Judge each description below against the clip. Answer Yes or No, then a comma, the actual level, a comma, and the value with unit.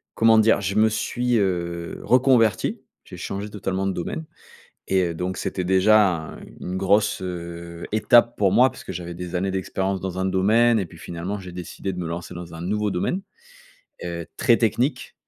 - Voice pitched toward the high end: No, very low, 95 Hz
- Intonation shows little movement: No, average, 3.3 semitones